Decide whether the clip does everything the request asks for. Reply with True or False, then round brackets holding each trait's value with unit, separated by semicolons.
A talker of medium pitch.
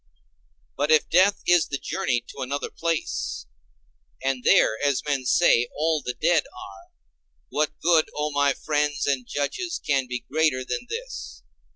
True (145 Hz)